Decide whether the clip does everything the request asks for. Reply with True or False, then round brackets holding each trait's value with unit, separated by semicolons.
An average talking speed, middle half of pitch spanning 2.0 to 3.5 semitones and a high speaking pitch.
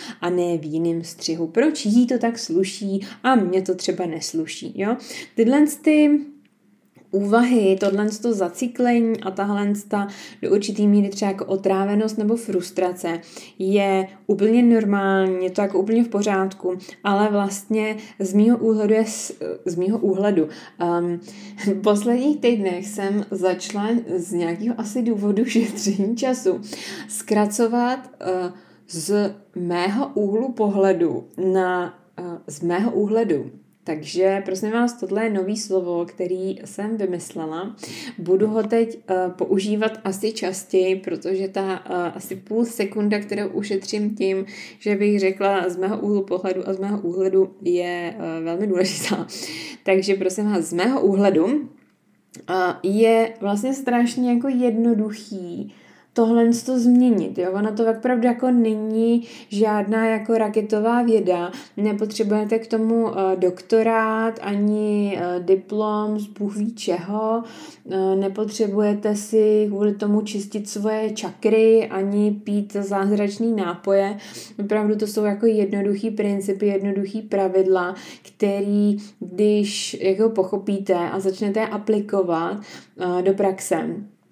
True (125 wpm; 2.6 semitones; 205 Hz)